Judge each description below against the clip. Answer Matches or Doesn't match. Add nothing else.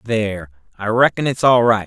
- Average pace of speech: Matches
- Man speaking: Matches